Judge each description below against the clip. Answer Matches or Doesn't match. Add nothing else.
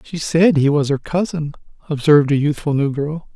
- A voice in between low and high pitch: Matches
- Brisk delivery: Doesn't match